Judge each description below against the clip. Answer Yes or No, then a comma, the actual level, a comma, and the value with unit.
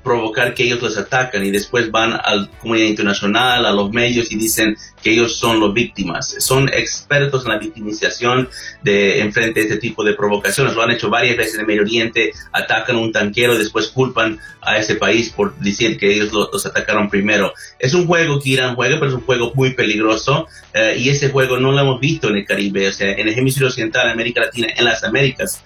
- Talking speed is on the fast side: Yes, fast, 225 wpm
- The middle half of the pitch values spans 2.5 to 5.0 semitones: Yes, average, 3.4 semitones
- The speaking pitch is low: Yes, low, 115 Hz